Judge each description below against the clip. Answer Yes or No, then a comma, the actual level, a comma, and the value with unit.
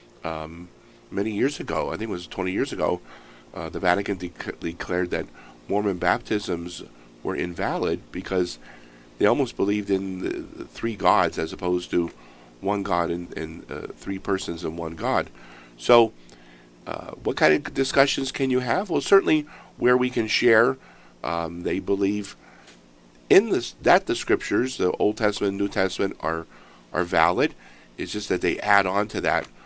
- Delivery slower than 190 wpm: Yes, average, 165 wpm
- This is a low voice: Yes, very low, 90 Hz